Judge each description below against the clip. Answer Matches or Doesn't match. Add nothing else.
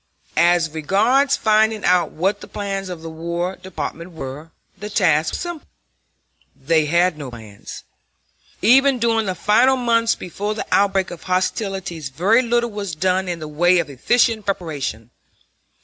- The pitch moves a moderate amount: Matches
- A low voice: Doesn't match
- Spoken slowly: Doesn't match